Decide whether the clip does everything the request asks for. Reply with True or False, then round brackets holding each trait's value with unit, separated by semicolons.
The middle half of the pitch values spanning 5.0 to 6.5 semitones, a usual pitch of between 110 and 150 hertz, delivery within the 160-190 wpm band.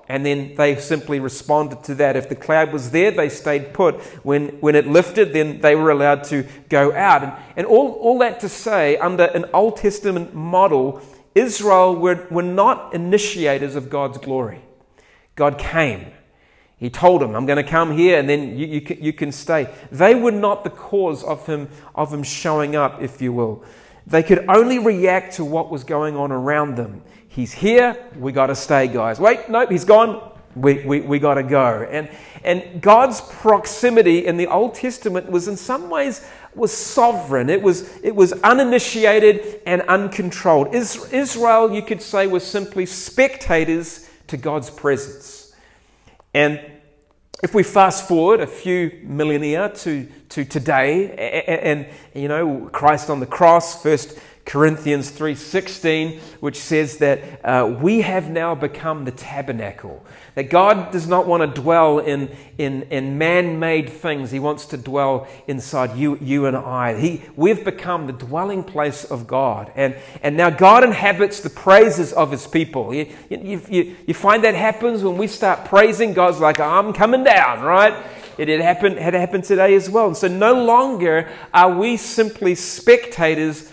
False (5.3 semitones; 165 Hz; 170 wpm)